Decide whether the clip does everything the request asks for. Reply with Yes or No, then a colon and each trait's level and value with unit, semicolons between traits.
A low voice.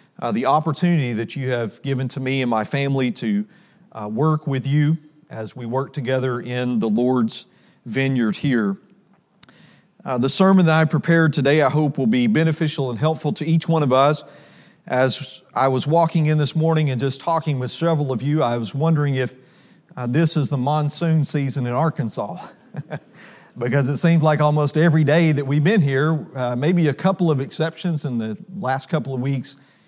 No: medium, 145 Hz